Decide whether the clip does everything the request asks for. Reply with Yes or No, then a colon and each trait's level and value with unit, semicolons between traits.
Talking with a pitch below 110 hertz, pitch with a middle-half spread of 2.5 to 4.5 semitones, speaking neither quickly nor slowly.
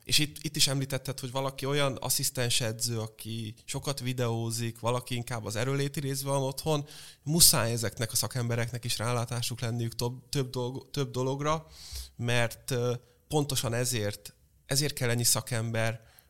No: low, 120 Hz; average, 2.9 semitones; average, 145 wpm